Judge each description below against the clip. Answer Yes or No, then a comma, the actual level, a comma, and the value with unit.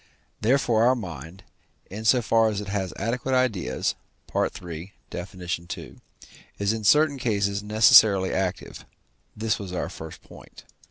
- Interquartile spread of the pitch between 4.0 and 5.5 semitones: No, average, 3.5 semitones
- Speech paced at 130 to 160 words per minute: Yes, average, 140 wpm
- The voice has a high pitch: No, low, 105 Hz